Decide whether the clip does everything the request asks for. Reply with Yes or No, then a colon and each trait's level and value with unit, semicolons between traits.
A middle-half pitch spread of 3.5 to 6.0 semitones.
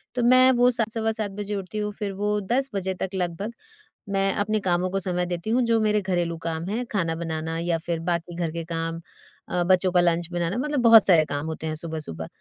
Yes: average, 4.1 semitones